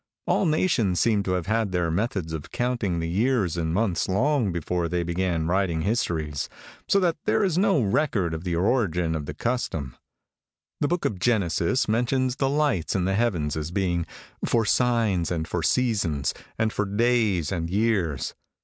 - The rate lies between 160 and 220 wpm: Yes, average, 175 wpm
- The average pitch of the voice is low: Yes, very low, 95 Hz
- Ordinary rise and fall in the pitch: No, wide, 6.0 semitones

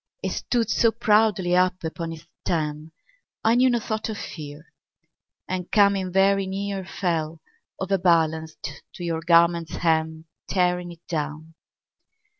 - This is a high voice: No, medium, 175 Hz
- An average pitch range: Yes, average, 3.4 semitones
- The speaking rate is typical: No, slow, 130 wpm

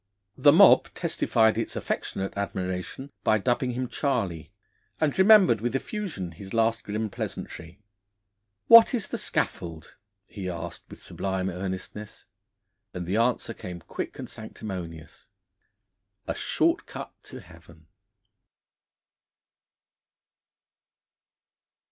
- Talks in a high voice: No, low, 105 Hz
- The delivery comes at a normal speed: No, slow, 105 wpm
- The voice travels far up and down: Yes, wide, 5.8 semitones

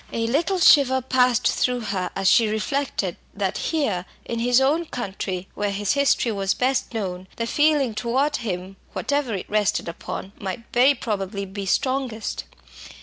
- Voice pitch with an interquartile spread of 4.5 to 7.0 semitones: Yes, average, 5.2 semitones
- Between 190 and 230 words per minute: No, average, 155 wpm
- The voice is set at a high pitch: Yes, high, 230 Hz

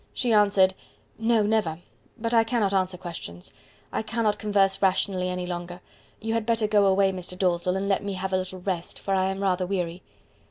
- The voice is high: Yes, high, 195 Hz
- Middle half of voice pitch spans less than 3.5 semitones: Yes, narrow, 2.5 semitones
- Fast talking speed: No, average, 195 wpm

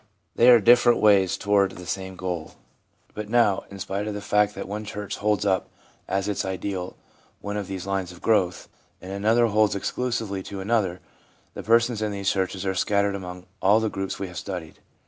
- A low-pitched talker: Yes, low, 100 Hz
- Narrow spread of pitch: Yes, narrow, 1.9 semitones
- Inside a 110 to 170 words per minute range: No, average, 195 wpm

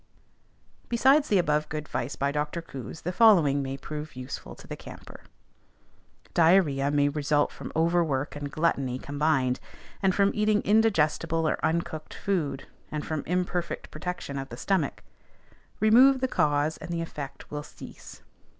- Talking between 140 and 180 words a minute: Yes, average, 150 wpm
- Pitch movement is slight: No, average, 3.9 semitones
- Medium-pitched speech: Yes, medium, 155 Hz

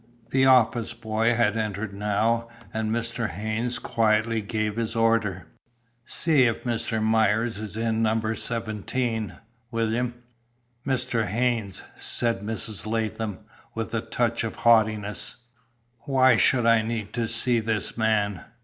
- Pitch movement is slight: Yes, narrow, 1.4 semitones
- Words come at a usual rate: No, slow, 130 wpm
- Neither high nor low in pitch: No, low, 115 Hz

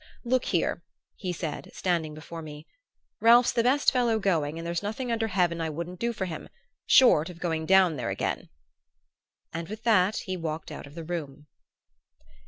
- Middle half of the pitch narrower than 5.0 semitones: No, wide, 5.4 semitones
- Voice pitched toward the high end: No, medium, 175 Hz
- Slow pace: No, average, 180 wpm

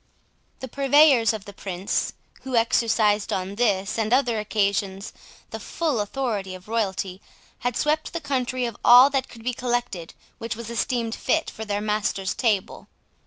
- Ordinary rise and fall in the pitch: Yes, average, 3.7 semitones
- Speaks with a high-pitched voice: Yes, high, 225 Hz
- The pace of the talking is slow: No, average, 160 wpm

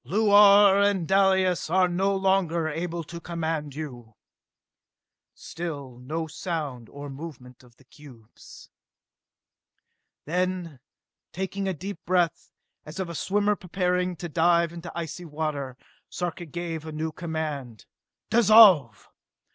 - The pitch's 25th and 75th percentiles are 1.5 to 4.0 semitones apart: Yes, average, 3.7 semitones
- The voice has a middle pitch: Yes, medium, 170 Hz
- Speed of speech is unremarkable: No, slow, 120 wpm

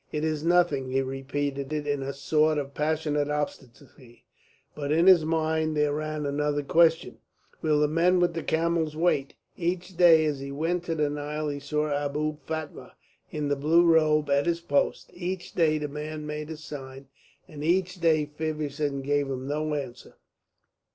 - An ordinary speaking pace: Yes, average, 170 wpm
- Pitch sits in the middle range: Yes, medium, 150 Hz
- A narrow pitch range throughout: Yes, narrow, 1.9 semitones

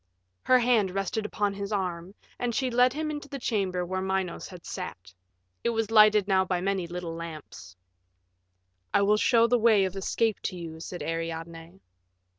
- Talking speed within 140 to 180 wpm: Yes, average, 175 wpm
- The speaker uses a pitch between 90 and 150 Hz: No, high, 195 Hz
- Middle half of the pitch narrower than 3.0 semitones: No, average, 4.2 semitones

